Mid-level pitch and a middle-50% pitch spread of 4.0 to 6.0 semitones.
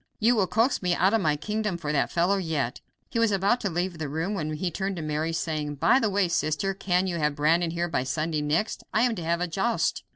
Yes: medium, 175 Hz; average, 4.3 semitones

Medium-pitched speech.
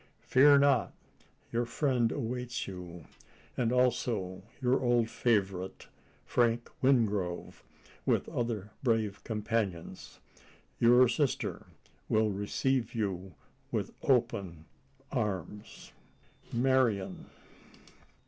No: low, 115 Hz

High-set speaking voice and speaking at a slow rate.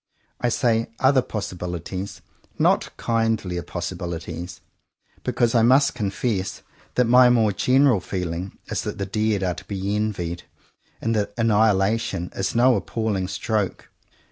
No: low, 105 Hz; slow, 130 wpm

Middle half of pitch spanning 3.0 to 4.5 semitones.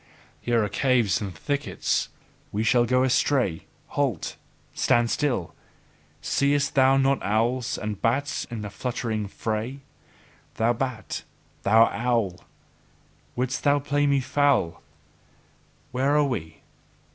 Yes: average, 3.9 semitones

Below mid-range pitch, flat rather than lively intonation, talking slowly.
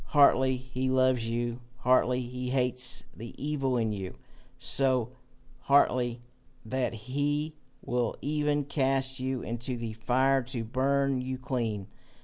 Yes: low, 130 Hz; narrow, 2.0 semitones; slow, 130 wpm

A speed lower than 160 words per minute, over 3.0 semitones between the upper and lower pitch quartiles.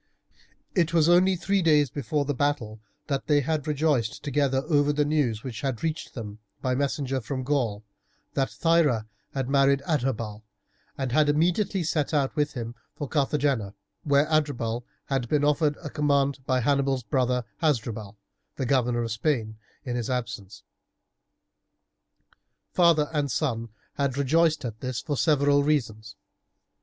Yes: average, 150 wpm; average, 3.6 semitones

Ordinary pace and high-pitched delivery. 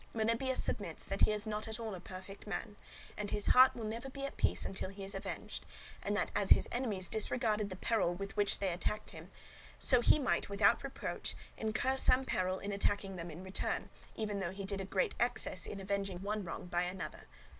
No: fast, 210 wpm; high, 205 Hz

